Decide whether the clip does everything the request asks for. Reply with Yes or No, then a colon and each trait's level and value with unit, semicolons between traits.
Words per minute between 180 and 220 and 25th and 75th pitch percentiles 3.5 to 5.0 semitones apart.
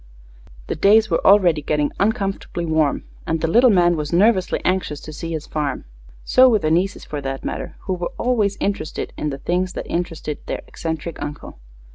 Yes: average, 185 wpm; average, 4.4 semitones